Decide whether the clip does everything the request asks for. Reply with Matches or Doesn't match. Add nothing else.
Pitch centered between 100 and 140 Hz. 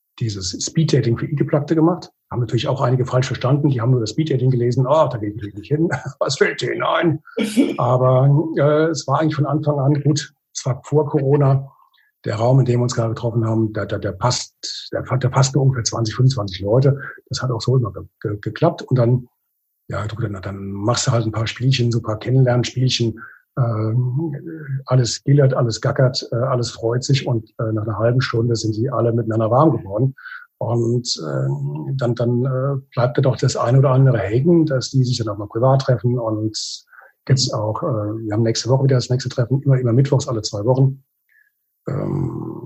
Matches